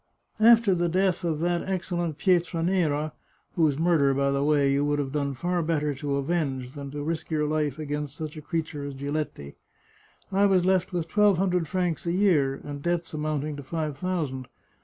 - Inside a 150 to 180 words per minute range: No, average, 190 wpm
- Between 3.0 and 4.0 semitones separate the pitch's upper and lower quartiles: Yes, average, 3.4 semitones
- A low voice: No, medium, 155 Hz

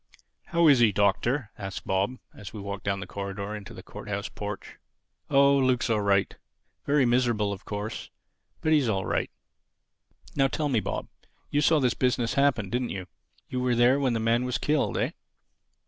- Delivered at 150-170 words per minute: No, average, 185 wpm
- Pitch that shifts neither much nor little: Yes, average, 4.9 semitones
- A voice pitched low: Yes, low, 120 Hz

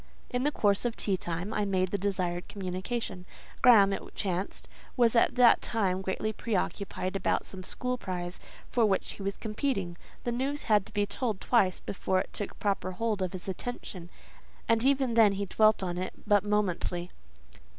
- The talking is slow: No, average, 180 wpm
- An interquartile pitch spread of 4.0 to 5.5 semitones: No, average, 3.5 semitones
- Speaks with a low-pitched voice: No, high, 200 Hz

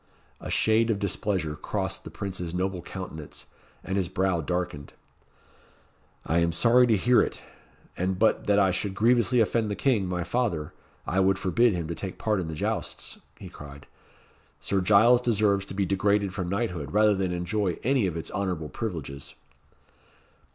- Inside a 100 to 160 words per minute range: No, average, 170 wpm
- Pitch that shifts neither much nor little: Yes, average, 3.4 semitones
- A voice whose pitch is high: No, very low, 95 Hz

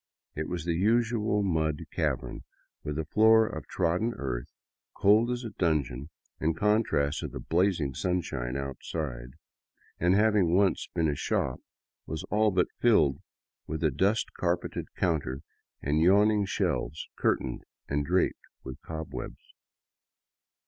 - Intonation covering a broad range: Yes, wide, 5.9 semitones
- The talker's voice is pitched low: Yes, very low, 85 Hz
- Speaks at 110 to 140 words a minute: Yes, slow, 135 wpm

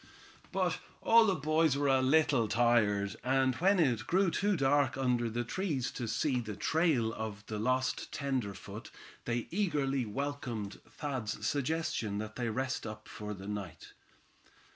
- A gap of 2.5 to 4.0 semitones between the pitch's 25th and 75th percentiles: No, average, 4.8 semitones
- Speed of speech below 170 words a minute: Yes, average, 150 wpm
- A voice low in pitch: Yes, low, 130 Hz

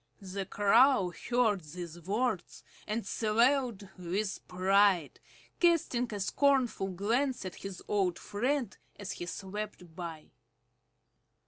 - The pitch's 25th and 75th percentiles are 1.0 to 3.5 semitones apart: No, average, 4.6 semitones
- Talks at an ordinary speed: No, slow, 110 wpm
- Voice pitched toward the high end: Yes, high, 205 Hz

